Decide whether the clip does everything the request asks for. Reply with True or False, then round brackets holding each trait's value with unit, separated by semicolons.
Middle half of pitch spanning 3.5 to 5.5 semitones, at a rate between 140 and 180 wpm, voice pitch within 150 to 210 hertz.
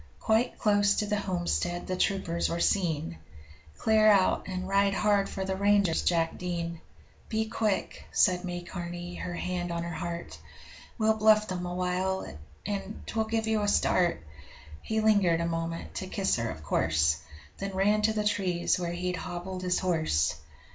False (2.9 semitones; 170 wpm; 185 Hz)